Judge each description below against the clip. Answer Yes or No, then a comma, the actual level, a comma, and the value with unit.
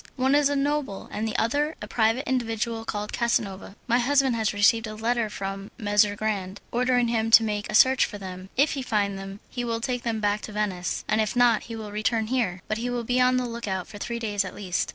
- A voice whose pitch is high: Yes, high, 225 Hz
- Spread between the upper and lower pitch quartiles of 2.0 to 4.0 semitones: Yes, average, 2.9 semitones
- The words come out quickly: Yes, fast, 240 wpm